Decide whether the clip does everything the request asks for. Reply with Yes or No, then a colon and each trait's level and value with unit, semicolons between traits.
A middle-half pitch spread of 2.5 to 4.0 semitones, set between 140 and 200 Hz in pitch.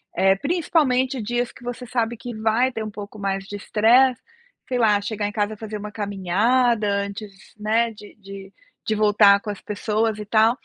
No: average, 2.8 semitones; high, 215 Hz